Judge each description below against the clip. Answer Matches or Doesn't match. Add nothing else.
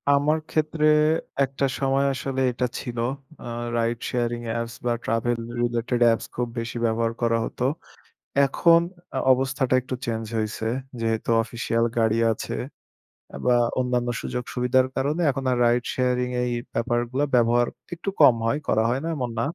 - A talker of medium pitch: Doesn't match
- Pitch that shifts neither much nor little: Doesn't match